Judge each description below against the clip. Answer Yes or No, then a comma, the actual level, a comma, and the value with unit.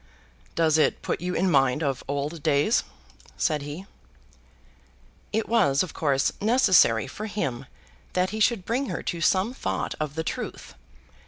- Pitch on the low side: No, medium, 165 Hz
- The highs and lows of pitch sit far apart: Yes, wide, 6.3 semitones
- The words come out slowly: No, average, 155 wpm